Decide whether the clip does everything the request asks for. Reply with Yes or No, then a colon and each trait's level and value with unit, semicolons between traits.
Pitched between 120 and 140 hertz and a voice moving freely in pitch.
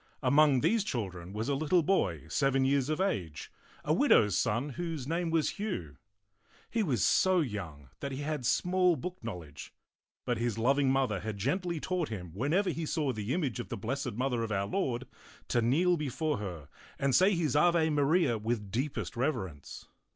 Yes: low, 135 Hz; wide, 6.8 semitones